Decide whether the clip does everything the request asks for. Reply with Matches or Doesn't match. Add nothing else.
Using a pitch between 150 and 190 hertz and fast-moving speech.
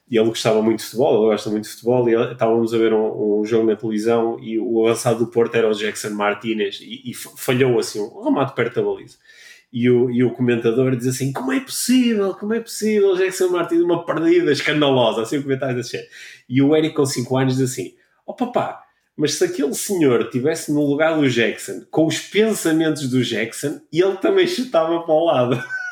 Doesn't match